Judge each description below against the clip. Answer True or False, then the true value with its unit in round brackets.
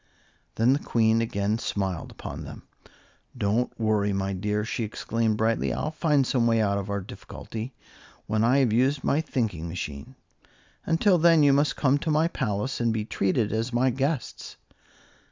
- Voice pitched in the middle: False (115 Hz)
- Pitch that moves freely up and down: False (4.5 semitones)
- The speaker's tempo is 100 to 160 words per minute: False (170 wpm)